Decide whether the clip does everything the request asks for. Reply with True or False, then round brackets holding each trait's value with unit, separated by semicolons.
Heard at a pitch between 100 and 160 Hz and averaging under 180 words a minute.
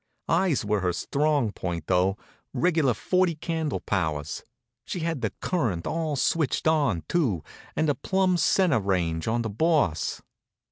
True (135 Hz; 145 wpm)